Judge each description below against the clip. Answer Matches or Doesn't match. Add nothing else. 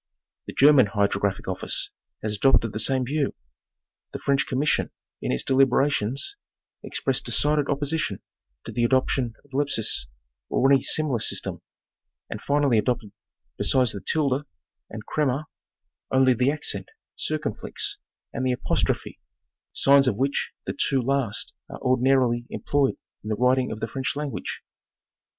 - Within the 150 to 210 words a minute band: Doesn't match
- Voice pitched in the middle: Doesn't match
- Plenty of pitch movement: Doesn't match